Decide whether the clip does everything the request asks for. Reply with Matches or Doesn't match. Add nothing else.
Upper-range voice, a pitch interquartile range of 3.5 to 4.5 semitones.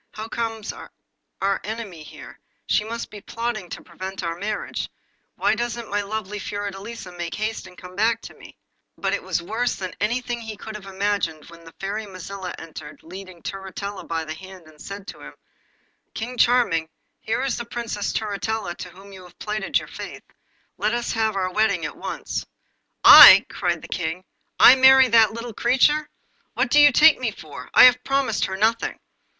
Matches